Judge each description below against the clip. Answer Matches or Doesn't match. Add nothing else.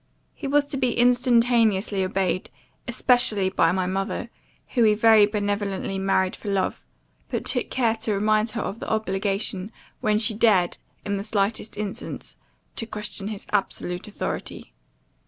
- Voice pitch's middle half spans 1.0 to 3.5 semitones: Matches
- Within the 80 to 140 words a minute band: Doesn't match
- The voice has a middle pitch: Doesn't match